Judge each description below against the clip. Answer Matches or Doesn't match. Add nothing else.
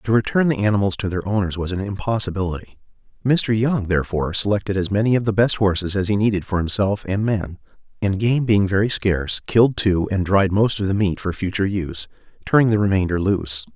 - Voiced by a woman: Doesn't match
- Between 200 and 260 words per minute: Matches